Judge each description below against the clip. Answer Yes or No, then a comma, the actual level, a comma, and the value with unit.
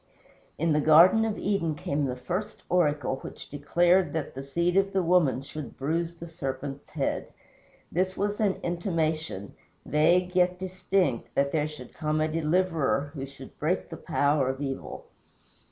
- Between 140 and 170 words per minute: Yes, average, 160 wpm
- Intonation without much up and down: No, average, 4.1 semitones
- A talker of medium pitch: Yes, medium, 160 Hz